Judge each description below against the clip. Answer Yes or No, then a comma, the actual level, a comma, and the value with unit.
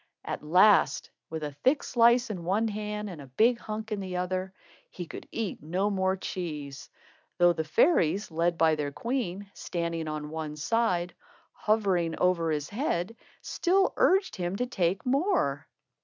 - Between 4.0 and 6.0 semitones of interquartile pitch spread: Yes, average, 5.1 semitones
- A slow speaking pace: No, average, 165 wpm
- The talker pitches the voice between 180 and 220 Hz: Yes, medium, 185 Hz